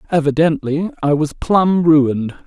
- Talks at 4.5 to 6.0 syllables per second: No, 4.3 syllables/s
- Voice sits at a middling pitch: Yes, medium, 155 Hz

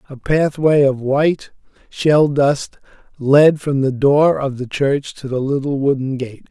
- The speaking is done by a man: Yes, male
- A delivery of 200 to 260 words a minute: No, average, 165 wpm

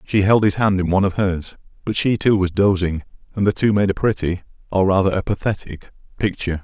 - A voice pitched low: Yes, very low, 95 Hz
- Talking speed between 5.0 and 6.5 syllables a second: Yes, 5.9 syllables/s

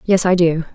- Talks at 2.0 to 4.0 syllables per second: No, 5.3 syllables/s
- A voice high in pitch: No, medium, 175 Hz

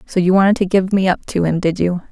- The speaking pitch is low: No, medium, 185 Hz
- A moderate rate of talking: No, fast, 310 wpm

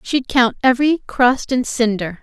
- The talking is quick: No, average, 160 wpm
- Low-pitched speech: No, high, 245 Hz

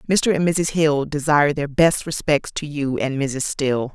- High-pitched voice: No, medium, 145 Hz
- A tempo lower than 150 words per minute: No, average, 200 wpm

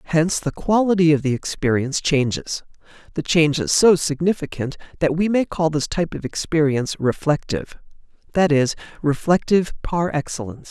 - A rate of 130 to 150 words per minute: Yes, average, 140 wpm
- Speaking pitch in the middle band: Yes, medium, 160 Hz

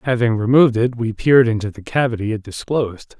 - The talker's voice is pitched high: No, low, 115 Hz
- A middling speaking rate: Yes, average, 190 wpm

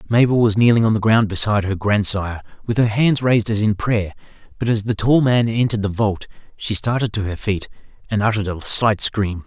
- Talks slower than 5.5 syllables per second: No, 5.8 syllables/s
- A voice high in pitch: No, low, 110 Hz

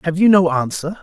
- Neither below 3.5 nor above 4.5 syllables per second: No, 5.6 syllables/s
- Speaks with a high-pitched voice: No, medium, 170 Hz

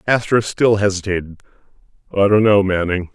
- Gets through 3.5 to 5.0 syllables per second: No, 5.3 syllables/s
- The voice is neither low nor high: No, low, 100 Hz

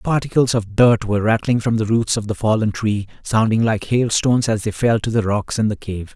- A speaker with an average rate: No, fast, 235 wpm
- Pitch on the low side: Yes, low, 110 Hz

